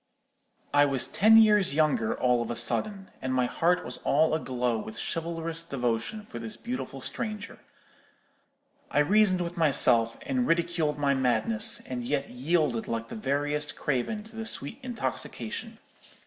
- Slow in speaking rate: No, average, 155 wpm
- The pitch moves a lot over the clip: Yes, wide, 8.5 semitones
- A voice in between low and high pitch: Yes, medium, 150 Hz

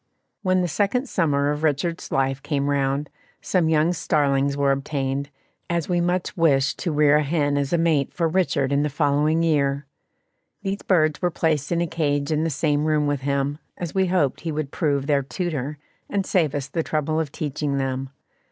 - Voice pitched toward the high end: No, medium, 150 Hz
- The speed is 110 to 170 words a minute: No, average, 195 wpm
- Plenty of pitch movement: No, average, 2.9 semitones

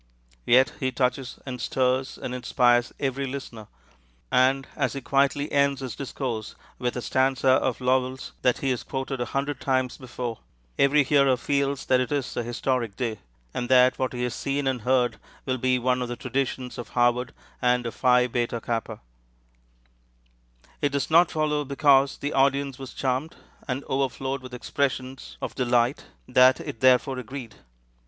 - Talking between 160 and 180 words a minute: Yes, average, 165 wpm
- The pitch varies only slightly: Yes, narrow, 1.7 semitones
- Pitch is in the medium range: No, low, 130 Hz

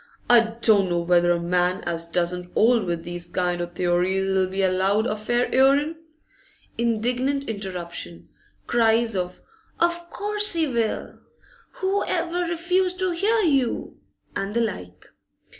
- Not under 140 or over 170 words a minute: Yes, average, 145 wpm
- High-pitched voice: Yes, high, 215 Hz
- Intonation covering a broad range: Yes, wide, 7.9 semitones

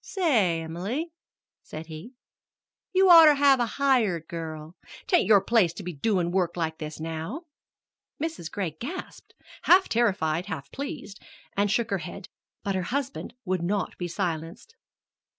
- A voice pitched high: Yes, high, 195 Hz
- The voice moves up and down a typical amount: No, wide, 8.2 semitones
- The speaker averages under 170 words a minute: Yes, average, 155 wpm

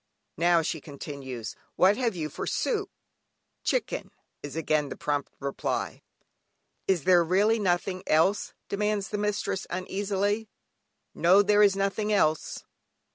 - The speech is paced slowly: Yes, slow, 130 wpm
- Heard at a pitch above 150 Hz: Yes, high, 190 Hz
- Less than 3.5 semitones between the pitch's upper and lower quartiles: No, average, 4.7 semitones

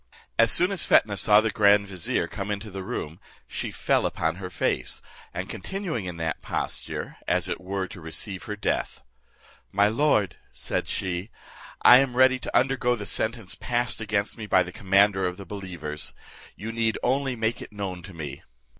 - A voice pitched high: No, low, 100 Hz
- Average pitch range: Yes, average, 3.8 semitones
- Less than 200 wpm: Yes, average, 180 wpm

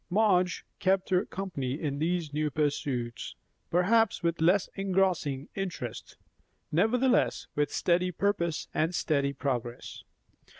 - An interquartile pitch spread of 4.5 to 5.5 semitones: Yes, average, 4.8 semitones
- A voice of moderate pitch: Yes, medium, 170 Hz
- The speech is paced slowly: Yes, slow, 115 wpm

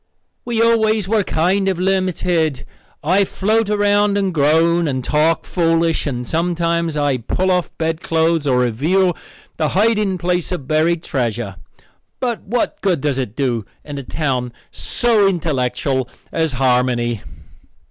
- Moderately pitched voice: Yes, medium, 165 Hz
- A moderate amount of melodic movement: No, wide, 5.8 semitones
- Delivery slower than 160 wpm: Yes, slow, 135 wpm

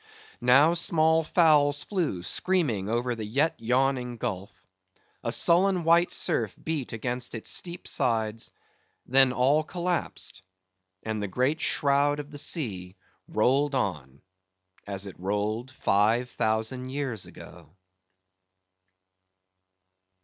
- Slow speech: Yes, slow, 115 wpm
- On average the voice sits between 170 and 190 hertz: No, low, 125 Hz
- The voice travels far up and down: Yes, wide, 5.9 semitones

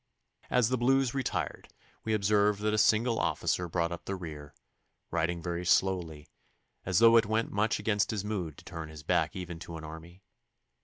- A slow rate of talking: No, average, 185 wpm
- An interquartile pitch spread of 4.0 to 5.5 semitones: Yes, average, 4.5 semitones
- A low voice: Yes, very low, 95 Hz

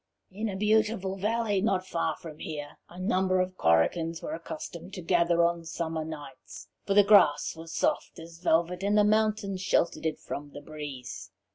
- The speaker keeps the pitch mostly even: No, average, 3.7 semitones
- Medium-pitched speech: Yes, medium, 175 Hz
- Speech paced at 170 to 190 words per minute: Yes, average, 175 wpm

